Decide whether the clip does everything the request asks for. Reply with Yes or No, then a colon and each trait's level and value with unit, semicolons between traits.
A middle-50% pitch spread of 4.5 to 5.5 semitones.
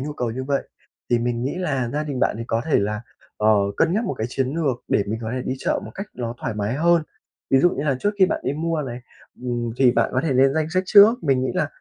Yes: average, 4.8 semitones